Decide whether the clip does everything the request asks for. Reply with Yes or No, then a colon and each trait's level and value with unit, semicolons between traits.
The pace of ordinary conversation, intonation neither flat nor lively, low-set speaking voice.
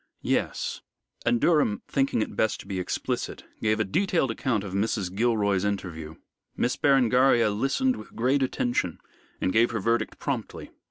Yes: average, 155 wpm; average, 4.3 semitones; low, 115 Hz